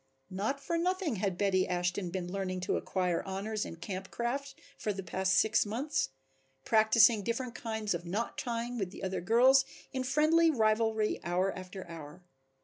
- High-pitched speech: Yes, high, 210 Hz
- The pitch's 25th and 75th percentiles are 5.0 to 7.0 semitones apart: No, average, 4.3 semitones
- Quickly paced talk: No, average, 165 wpm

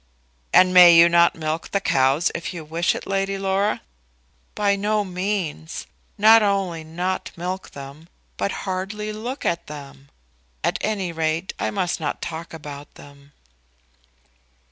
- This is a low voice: No, medium, 175 Hz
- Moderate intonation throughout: Yes, average, 3.8 semitones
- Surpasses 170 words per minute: No, average, 145 wpm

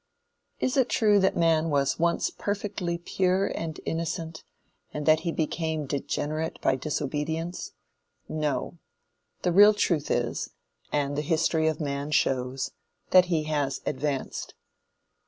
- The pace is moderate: No, slow, 130 wpm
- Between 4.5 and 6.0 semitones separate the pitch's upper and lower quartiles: No, average, 2.8 semitones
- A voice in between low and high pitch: Yes, medium, 160 Hz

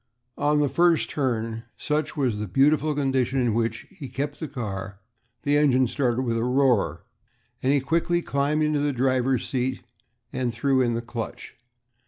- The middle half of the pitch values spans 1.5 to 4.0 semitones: Yes, average, 3.5 semitones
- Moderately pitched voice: No, low, 130 Hz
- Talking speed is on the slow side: No, average, 170 wpm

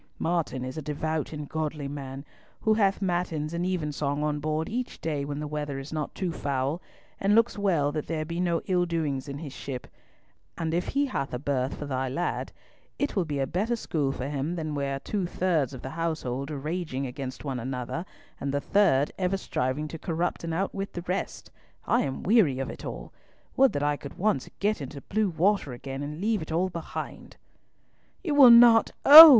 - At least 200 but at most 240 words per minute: Yes, fast, 205 wpm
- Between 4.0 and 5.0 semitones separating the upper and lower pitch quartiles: Yes, average, 4.5 semitones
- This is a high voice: No, medium, 155 Hz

